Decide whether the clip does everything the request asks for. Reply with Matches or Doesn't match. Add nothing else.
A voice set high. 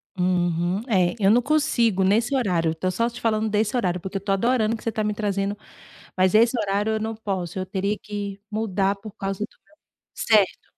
Matches